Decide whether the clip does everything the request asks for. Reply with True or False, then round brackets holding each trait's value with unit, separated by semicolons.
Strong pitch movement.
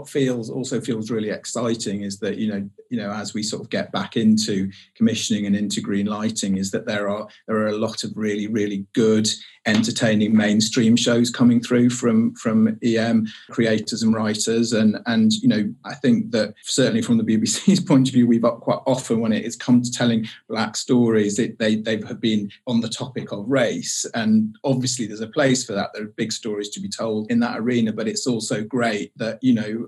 False (3.5 semitones)